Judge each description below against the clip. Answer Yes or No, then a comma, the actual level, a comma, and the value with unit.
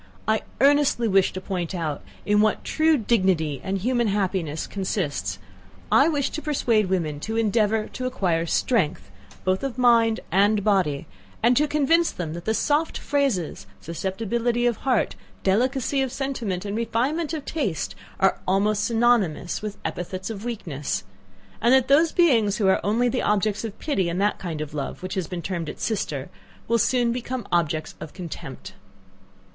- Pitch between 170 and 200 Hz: No, high, 210 Hz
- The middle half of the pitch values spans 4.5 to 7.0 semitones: Yes, average, 5.2 semitones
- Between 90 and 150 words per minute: No, average, 165 wpm